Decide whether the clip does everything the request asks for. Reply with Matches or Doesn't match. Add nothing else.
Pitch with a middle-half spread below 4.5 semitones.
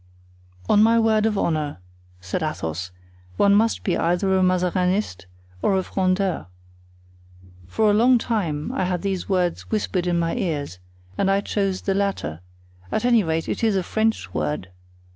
Matches